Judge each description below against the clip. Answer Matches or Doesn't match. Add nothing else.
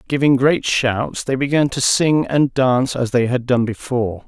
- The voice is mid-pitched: Doesn't match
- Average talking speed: Matches